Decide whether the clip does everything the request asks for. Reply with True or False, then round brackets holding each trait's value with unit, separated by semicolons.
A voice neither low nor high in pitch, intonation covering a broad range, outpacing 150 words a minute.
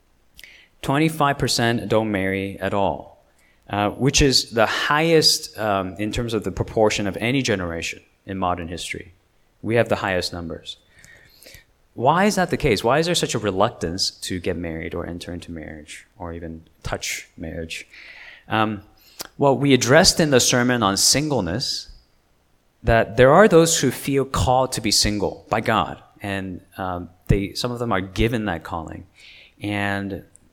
False (105 Hz; 5.9 semitones; 165 wpm)